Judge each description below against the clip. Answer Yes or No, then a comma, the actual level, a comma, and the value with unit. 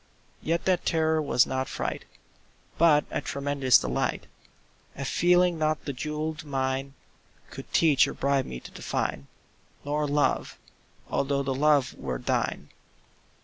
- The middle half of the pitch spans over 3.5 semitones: No, average, 2.7 semitones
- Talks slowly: Yes, slow, 130 wpm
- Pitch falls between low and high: Yes, medium, 145 Hz